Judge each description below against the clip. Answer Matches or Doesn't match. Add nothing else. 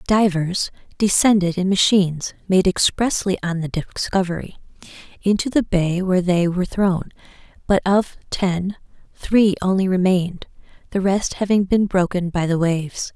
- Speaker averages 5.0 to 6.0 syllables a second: Doesn't match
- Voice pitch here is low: Doesn't match